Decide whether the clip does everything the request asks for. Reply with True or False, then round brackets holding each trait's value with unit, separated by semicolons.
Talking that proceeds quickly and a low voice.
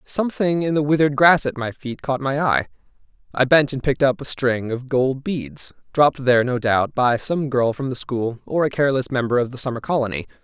True (225 wpm; 130 Hz)